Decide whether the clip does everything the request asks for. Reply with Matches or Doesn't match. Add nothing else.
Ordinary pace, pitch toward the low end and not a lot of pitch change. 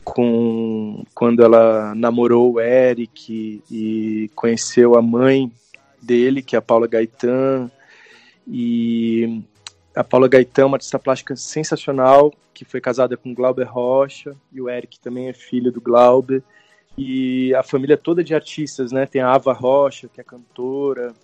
Matches